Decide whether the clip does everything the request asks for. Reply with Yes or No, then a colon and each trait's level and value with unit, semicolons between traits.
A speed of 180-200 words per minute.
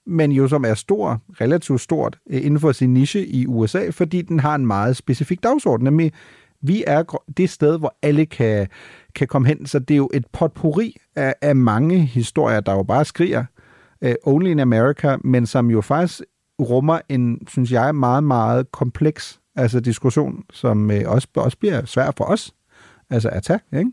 Yes: average, 185 wpm